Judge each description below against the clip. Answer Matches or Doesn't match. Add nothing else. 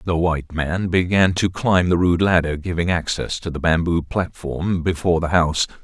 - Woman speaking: Doesn't match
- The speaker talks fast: Doesn't match